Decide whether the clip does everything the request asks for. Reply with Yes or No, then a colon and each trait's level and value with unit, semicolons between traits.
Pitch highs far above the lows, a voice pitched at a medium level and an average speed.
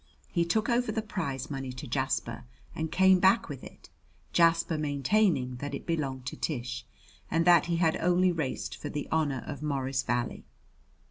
No: average, 4.7 semitones; medium, 155 Hz; average, 175 wpm